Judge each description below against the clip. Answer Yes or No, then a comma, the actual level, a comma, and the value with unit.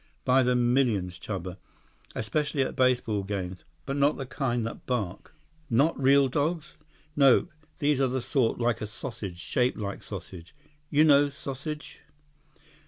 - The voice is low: Yes, low, 125 Hz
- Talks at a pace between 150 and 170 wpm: No, average, 140 wpm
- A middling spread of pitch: Yes, average, 4.6 semitones